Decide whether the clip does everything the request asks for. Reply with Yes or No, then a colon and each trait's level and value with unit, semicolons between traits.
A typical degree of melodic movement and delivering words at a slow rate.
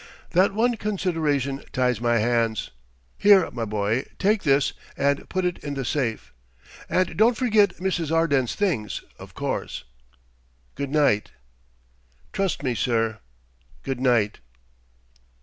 No: wide, 7.6 semitones; slow, 125 wpm